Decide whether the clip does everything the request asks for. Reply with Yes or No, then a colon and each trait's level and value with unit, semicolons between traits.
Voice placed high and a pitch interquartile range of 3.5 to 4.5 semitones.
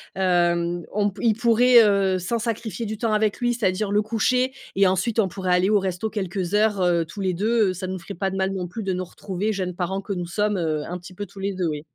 No: high, 195 Hz; average, 2.9 semitones